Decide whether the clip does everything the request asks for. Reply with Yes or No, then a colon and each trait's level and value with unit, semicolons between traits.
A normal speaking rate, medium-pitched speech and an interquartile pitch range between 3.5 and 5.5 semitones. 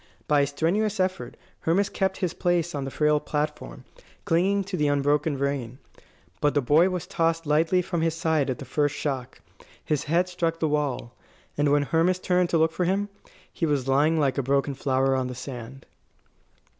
Yes: average, 190 wpm; medium, 150 Hz; average, 3.8 semitones